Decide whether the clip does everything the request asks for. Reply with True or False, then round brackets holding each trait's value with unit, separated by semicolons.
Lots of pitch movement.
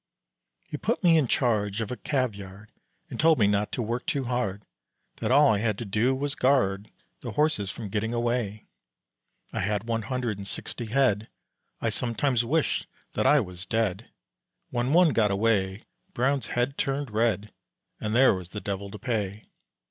False (4.1 semitones)